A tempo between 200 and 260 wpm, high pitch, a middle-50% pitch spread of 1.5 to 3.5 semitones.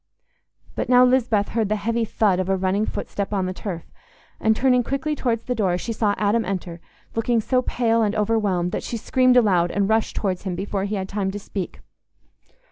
Yes: fast, 205 wpm; high, 210 Hz; average, 3.2 semitones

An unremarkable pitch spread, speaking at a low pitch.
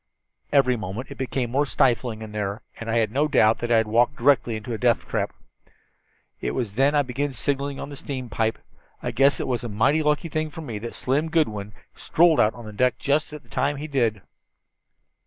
Yes: average, 4.2 semitones; low, 125 Hz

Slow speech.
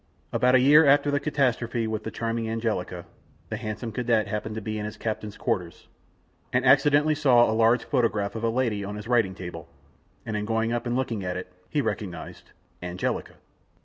No: average, 185 wpm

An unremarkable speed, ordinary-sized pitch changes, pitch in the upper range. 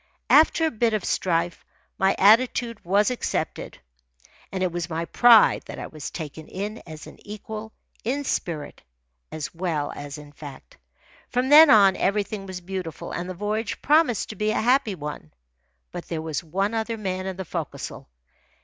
Yes: average, 170 wpm; average, 4.9 semitones; high, 195 Hz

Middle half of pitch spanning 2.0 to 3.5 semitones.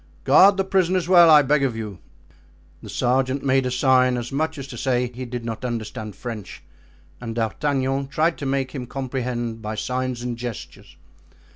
Yes: narrow, 2.6 semitones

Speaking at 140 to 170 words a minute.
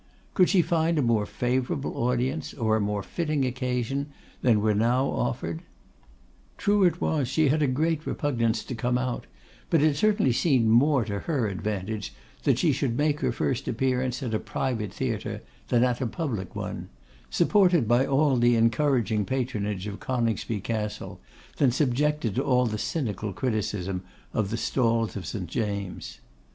Yes: average, 165 wpm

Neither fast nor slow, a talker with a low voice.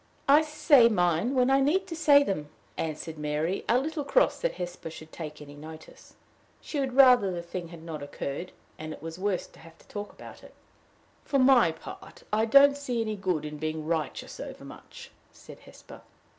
No: average, 190 wpm; medium, 185 Hz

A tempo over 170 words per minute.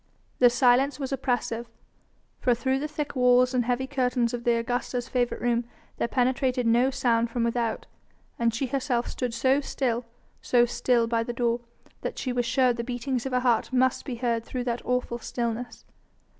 Yes: average, 185 wpm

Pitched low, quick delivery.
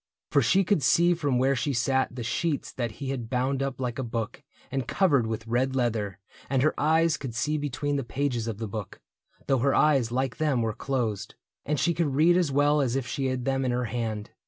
Yes: low, 130 Hz; fast, 230 wpm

